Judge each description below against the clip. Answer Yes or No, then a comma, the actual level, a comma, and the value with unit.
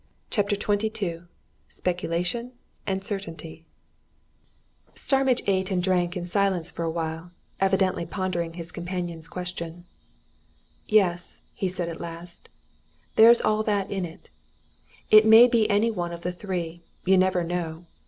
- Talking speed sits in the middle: No, slow, 130 wpm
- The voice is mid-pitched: Yes, medium, 180 Hz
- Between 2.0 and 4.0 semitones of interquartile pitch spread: Yes, average, 2.9 semitones